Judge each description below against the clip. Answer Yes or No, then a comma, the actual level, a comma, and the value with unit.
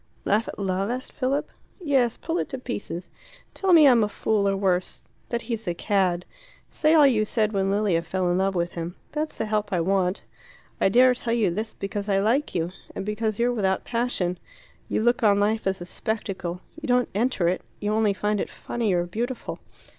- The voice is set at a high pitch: Yes, high, 210 Hz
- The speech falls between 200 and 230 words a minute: Yes, fast, 205 wpm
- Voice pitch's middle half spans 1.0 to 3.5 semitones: No, average, 4.1 semitones